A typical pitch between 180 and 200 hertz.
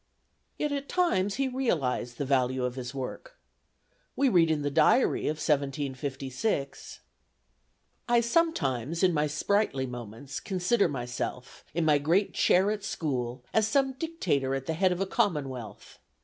No: medium, 150 Hz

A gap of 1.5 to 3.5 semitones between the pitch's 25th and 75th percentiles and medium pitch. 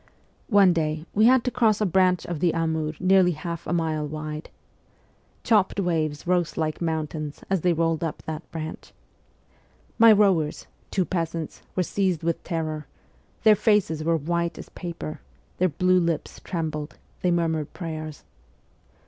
Yes: average, 2.7 semitones; medium, 165 Hz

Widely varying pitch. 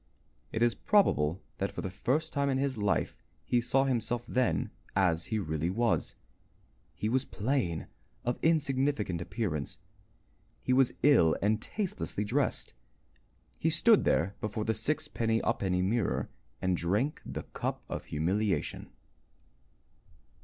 Yes: wide, 6.1 semitones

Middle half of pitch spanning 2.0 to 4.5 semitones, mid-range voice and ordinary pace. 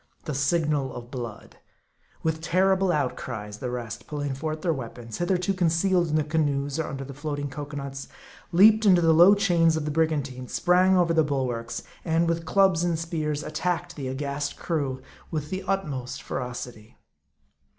Yes: average, 4.0 semitones; medium, 155 Hz; average, 170 wpm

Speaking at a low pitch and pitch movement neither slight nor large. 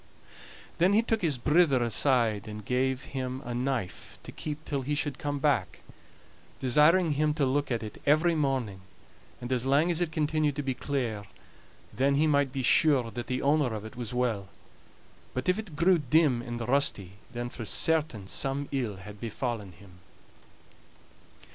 Yes: low, 130 Hz; average, 4.0 semitones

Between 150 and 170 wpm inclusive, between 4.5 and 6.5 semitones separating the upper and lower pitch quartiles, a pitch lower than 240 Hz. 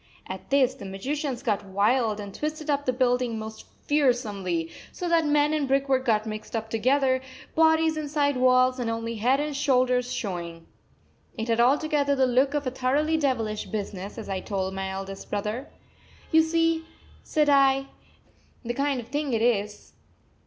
No: average, 165 wpm; average, 4.9 semitones; very high, 255 Hz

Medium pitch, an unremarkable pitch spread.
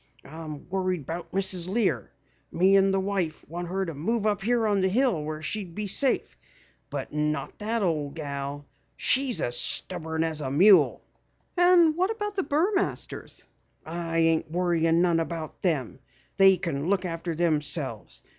Yes: medium, 175 Hz; average, 4.4 semitones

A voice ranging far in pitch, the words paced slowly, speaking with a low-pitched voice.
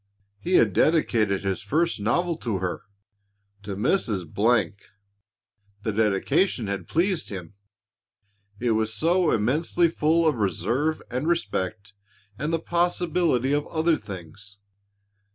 Yes: wide, 8.3 semitones; slow, 120 wpm; low, 115 Hz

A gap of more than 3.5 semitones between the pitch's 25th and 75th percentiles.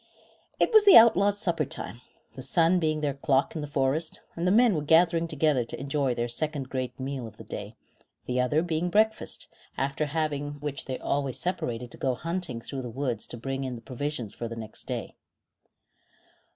Yes: average, 4.5 semitones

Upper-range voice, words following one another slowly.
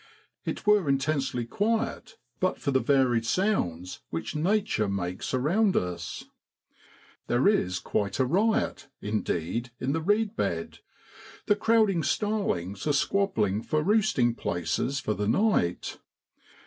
No: medium, 140 Hz; slow, 130 wpm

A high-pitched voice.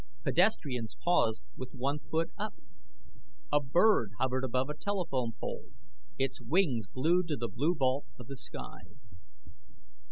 No: low, 135 Hz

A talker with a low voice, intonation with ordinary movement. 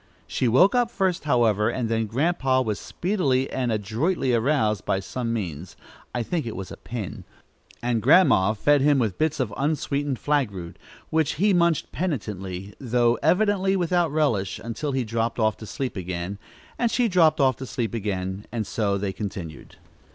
No: low, 120 Hz; wide, 6.4 semitones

